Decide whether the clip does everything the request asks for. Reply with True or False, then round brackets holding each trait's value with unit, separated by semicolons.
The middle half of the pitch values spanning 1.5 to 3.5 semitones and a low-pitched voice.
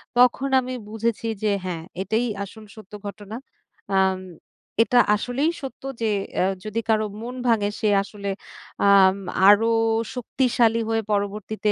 False (2.7 semitones; 220 Hz)